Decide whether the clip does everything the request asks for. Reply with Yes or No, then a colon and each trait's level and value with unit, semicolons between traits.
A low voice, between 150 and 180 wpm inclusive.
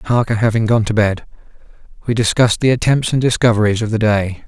Yes: low, 110 Hz; average, 175 wpm